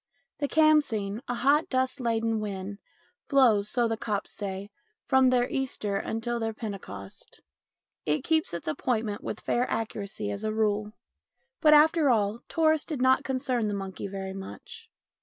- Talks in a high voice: Yes, high, 225 Hz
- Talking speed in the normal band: Yes, average, 155 wpm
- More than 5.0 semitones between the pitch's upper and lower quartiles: No, average, 4.5 semitones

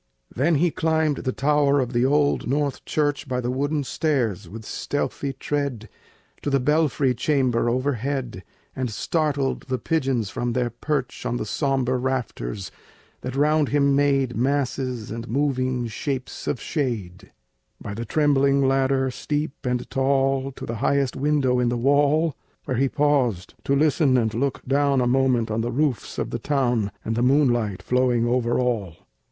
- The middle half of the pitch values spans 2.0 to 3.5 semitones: Yes, average, 2.9 semitones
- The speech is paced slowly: No, average, 160 wpm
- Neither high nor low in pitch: No, low, 130 Hz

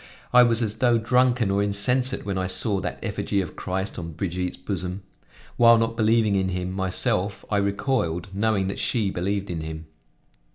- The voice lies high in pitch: No, low, 100 Hz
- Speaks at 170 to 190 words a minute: Yes, average, 175 wpm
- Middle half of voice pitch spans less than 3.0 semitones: No, average, 3.5 semitones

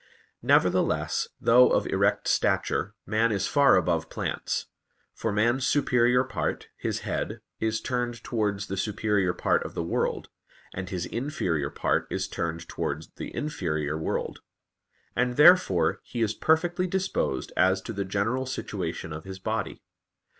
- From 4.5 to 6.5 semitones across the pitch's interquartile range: Yes, average, 5.2 semitones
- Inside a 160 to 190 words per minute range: No, average, 145 wpm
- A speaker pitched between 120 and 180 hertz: No, low, 110 Hz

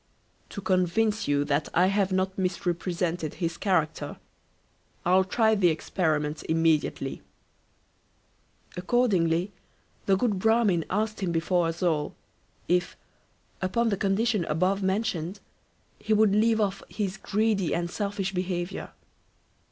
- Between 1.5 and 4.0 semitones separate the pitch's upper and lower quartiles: Yes, average, 3.3 semitones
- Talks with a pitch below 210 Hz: Yes, medium, 185 Hz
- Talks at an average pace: No, slow, 120 wpm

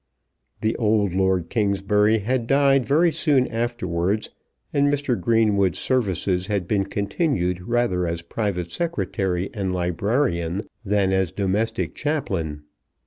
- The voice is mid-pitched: No, low, 100 Hz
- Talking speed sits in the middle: No, slow, 120 wpm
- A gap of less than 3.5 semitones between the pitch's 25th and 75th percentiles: No, average, 4.7 semitones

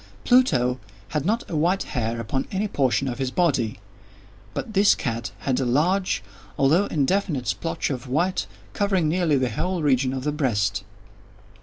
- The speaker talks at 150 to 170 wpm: Yes, average, 160 wpm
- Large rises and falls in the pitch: Yes, wide, 6.3 semitones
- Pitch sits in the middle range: Yes, medium, 145 Hz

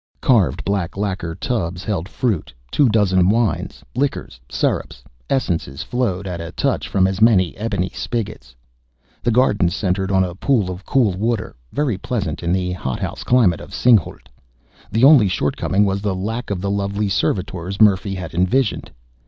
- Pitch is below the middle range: Yes, low, 100 Hz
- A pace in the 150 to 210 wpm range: Yes, average, 160 wpm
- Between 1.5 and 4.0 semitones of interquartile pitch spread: Yes, average, 3.7 semitones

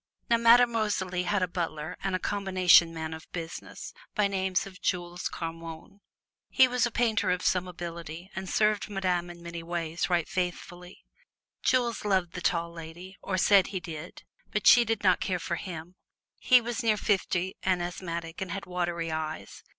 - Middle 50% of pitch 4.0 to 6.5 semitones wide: No, average, 2.8 semitones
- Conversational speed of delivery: Yes, average, 175 wpm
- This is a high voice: No, medium, 180 Hz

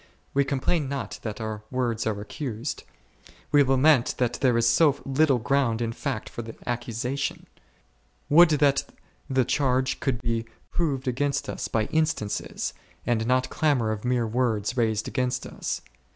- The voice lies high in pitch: No, low, 125 Hz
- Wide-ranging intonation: No, average, 3.4 semitones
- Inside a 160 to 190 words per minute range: No, average, 150 wpm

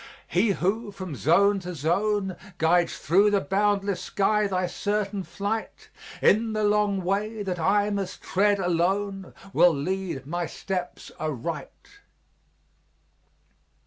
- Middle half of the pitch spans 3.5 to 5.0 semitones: No, narrow, 2.6 semitones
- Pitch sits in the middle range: No, high, 195 Hz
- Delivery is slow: Yes, slow, 120 wpm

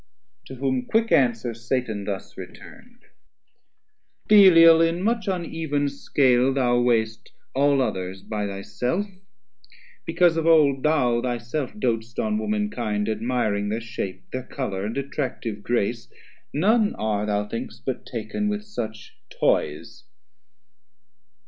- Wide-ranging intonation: Yes, wide, 6.8 semitones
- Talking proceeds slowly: Yes, slow, 125 wpm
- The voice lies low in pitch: Yes, low, 125 Hz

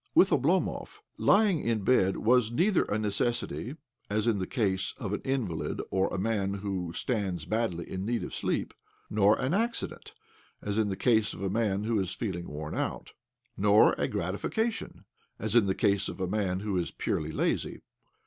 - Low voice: Yes, low, 105 Hz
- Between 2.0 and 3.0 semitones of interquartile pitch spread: No, average, 3.5 semitones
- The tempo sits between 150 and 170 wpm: No, average, 185 wpm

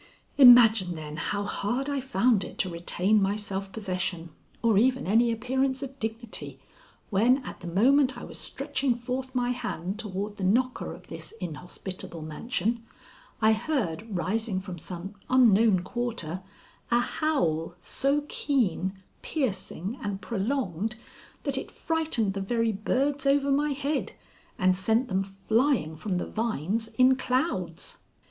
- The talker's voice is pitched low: No, high, 220 Hz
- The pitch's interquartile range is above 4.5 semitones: Yes, average, 5.2 semitones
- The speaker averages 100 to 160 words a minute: Yes, average, 140 wpm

